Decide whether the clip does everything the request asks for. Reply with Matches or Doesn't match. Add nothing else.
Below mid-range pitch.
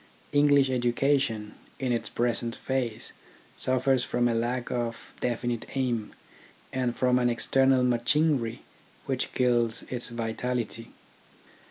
Matches